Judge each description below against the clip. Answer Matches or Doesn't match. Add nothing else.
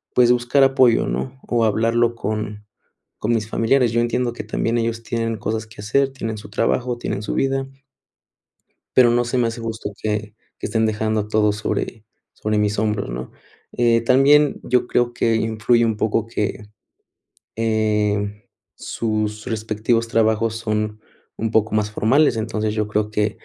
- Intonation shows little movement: Matches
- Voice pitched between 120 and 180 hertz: Doesn't match